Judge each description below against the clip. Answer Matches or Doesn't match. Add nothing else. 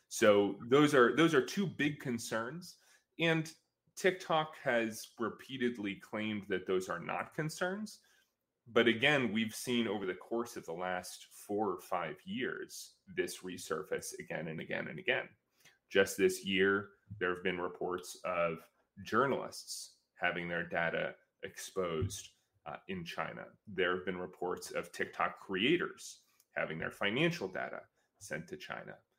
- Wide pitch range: Matches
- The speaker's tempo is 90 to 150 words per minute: Matches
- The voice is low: Matches